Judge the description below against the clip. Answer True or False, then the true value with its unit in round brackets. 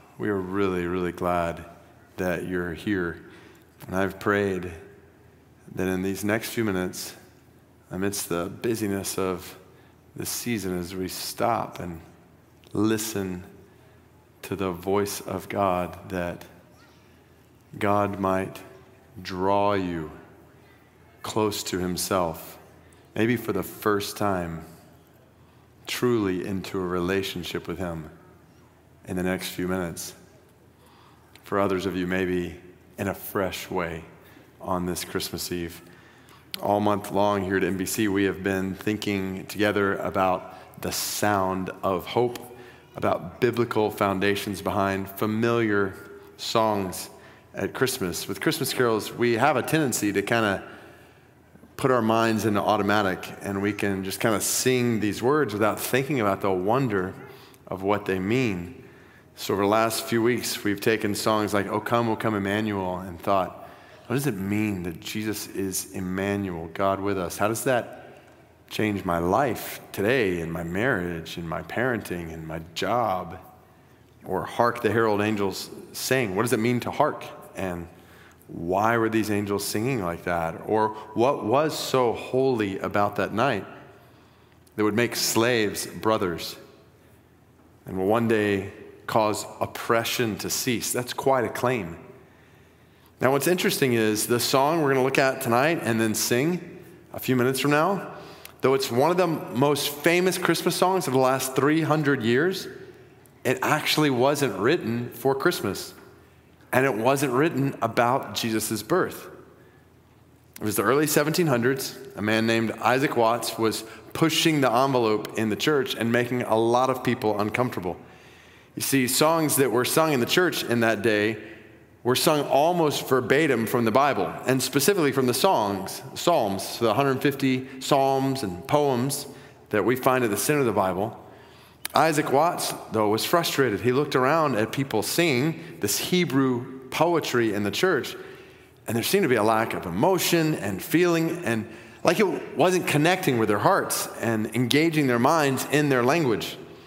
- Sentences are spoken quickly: False (150 wpm)